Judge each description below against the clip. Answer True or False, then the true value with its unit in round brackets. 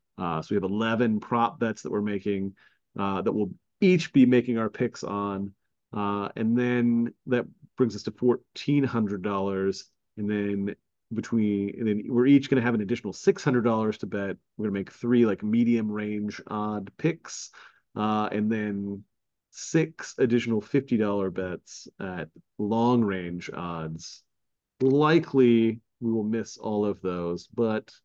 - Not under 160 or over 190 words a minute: False (150 wpm)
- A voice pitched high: False (110 Hz)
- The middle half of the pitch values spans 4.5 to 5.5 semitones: False (3.1 semitones)